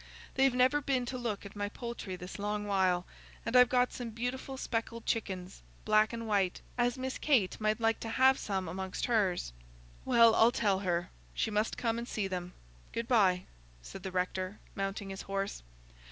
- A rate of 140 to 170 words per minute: No, average, 185 wpm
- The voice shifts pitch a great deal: No, average, 3.9 semitones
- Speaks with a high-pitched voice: Yes, high, 215 Hz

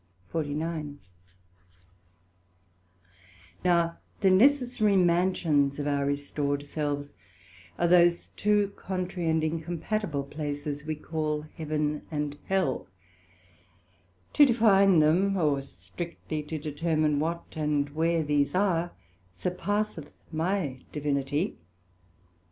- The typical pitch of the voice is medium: Yes, medium, 160 Hz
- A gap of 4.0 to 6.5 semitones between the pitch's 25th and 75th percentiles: No, average, 3.6 semitones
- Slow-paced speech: Yes, slow, 95 wpm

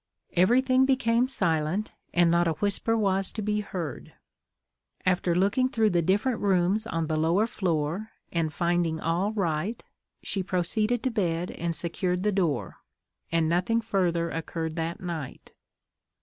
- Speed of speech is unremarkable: Yes, average, 145 wpm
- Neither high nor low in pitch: Yes, medium, 180 Hz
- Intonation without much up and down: No, average, 4.2 semitones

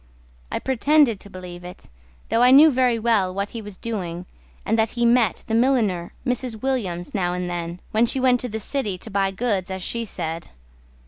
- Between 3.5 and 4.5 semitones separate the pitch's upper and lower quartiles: No, average, 5.1 semitones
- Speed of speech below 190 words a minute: No, average, 200 wpm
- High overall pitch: Yes, high, 220 Hz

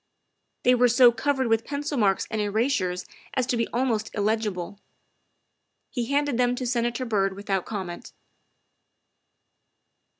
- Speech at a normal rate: No, slow, 130 wpm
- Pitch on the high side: Yes, high, 230 Hz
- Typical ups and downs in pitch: Yes, average, 3.6 semitones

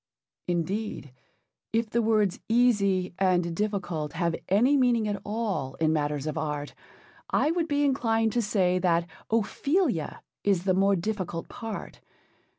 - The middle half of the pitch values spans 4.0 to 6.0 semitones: Yes, average, 4.9 semitones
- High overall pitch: Yes, high, 200 Hz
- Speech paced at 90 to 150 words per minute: Yes, average, 140 wpm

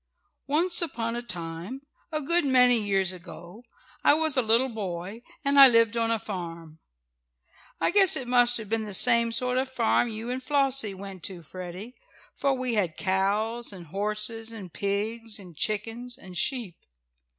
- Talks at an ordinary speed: Yes, average, 175 wpm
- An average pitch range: Yes, average, 4.5 semitones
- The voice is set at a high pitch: Yes, high, 225 Hz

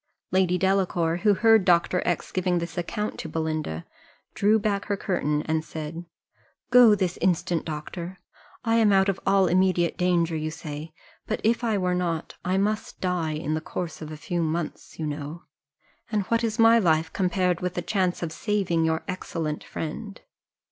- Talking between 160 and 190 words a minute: Yes, average, 175 wpm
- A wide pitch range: No, average, 3.5 semitones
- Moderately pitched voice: Yes, medium, 180 Hz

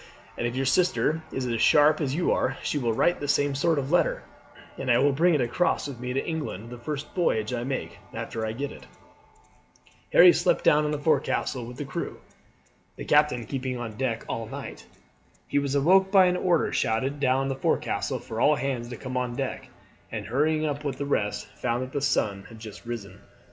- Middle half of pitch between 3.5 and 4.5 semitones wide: Yes, average, 3.8 semitones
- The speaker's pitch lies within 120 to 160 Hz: Yes, low, 135 Hz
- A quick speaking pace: Yes, fast, 210 wpm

